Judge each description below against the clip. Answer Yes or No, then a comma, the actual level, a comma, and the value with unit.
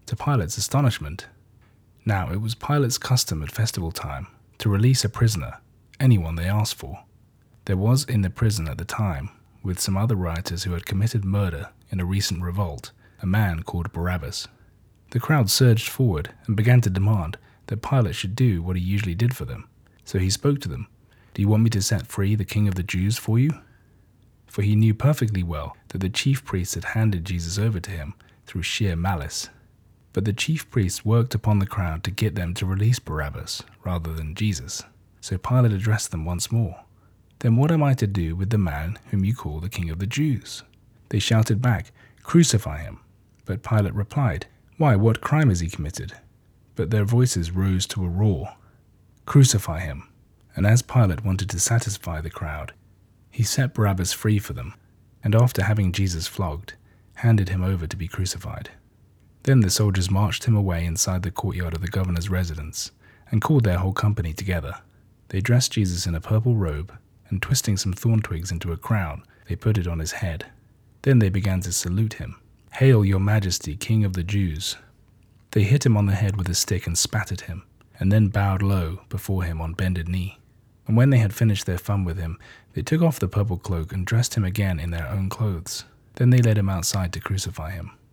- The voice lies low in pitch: Yes, low, 105 Hz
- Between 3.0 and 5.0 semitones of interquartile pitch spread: Yes, average, 3.5 semitones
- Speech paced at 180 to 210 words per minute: Yes, average, 200 wpm